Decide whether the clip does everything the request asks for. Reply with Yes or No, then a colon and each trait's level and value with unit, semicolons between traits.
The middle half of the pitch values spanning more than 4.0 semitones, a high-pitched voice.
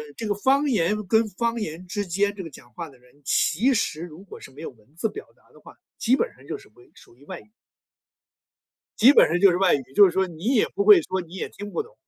Yes: average, 5.2 semitones; high, 195 Hz